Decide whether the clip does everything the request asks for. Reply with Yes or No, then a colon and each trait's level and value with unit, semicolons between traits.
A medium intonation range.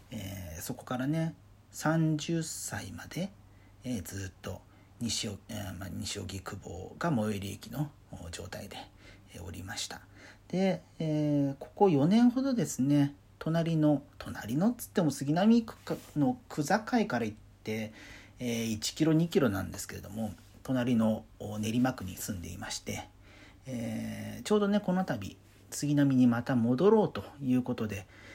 No: wide, 6.4 semitones